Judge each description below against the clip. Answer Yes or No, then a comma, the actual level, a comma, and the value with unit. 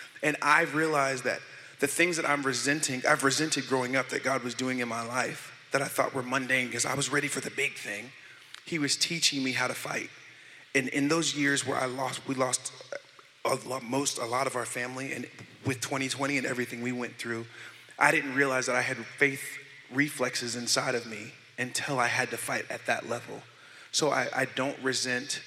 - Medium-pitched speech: No, low, 130 Hz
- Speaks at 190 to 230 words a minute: Yes, average, 200 wpm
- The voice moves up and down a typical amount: No, narrow, 2.1 semitones